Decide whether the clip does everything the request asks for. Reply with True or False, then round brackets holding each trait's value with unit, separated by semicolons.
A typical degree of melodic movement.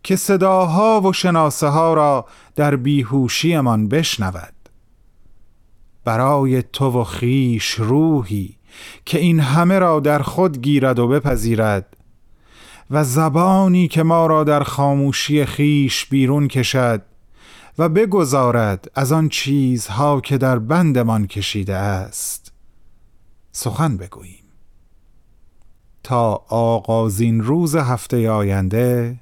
False (5.8 semitones)